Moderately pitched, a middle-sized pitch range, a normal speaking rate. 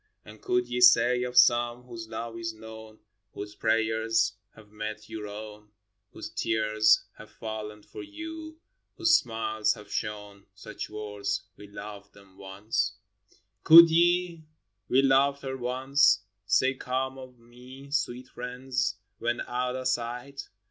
No: low, 115 Hz; average, 3.3 semitones; average, 145 wpm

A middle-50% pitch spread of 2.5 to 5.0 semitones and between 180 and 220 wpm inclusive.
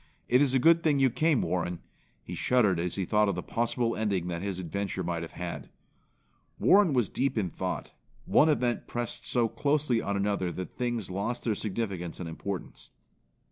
No: wide, 5.4 semitones; average, 185 wpm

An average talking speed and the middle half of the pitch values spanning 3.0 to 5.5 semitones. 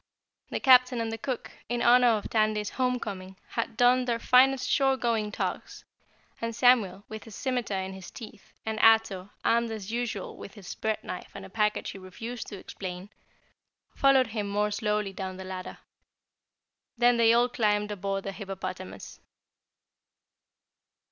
Yes: average, 155 wpm; average, 3.5 semitones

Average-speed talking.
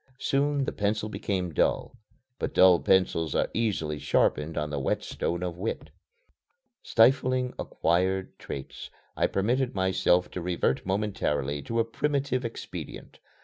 No: slow, 130 wpm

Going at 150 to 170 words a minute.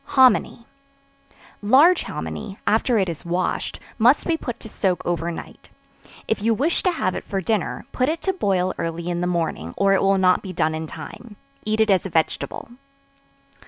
No: average, 190 wpm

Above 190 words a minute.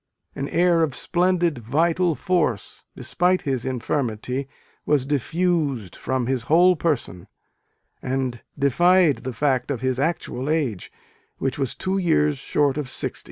No: slow, 135 wpm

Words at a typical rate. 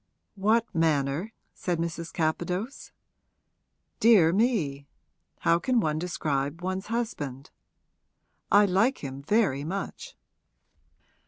No: slow, 95 wpm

